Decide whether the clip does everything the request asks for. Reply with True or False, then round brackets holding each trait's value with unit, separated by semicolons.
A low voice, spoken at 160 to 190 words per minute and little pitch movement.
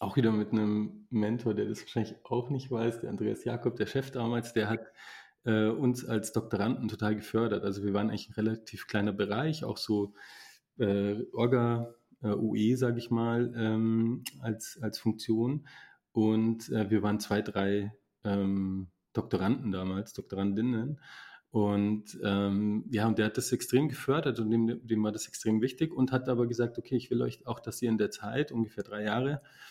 True (110 Hz; 180 wpm; 2.3 semitones)